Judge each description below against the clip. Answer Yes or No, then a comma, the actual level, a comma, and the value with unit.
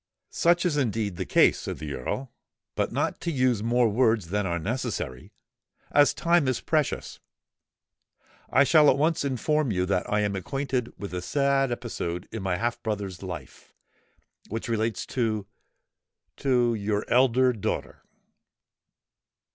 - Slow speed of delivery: Yes, slow, 130 wpm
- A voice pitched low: Yes, low, 115 Hz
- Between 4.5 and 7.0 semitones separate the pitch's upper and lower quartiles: Yes, average, 5.0 semitones